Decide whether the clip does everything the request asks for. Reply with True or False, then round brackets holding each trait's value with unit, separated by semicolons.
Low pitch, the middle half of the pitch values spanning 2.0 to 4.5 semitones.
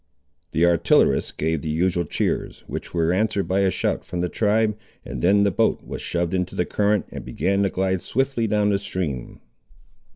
True (95 Hz; 3.0 semitones)